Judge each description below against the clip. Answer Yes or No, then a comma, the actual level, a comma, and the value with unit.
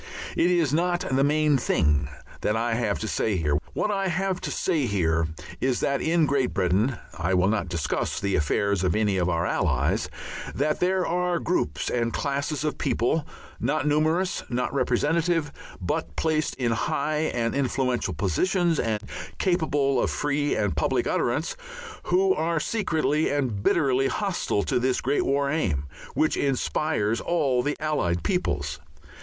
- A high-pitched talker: No, low, 135 Hz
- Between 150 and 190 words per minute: Yes, average, 155 wpm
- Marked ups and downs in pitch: Yes, wide, 7.4 semitones